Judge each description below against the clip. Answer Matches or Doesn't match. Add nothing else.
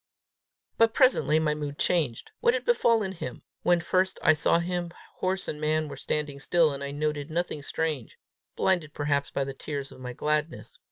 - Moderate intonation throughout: Matches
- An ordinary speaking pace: Matches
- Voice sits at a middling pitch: Matches